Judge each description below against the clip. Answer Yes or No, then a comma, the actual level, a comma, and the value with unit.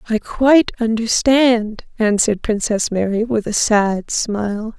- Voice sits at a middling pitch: No, high, 220 Hz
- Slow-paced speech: Yes, slow, 125 wpm